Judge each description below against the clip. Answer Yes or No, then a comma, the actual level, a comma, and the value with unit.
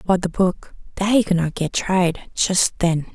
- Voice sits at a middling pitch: Yes, medium, 180 Hz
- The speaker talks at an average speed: Yes, average, 190 wpm